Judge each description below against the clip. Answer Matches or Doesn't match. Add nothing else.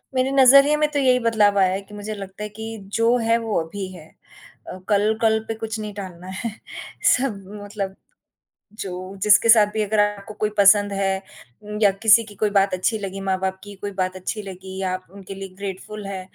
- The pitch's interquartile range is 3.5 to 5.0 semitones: Doesn't match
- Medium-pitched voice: Doesn't match